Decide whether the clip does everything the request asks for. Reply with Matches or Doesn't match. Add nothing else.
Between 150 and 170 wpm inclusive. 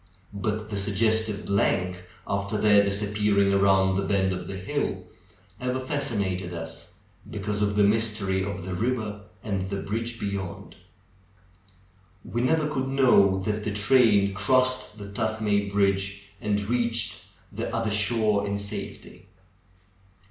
Doesn't match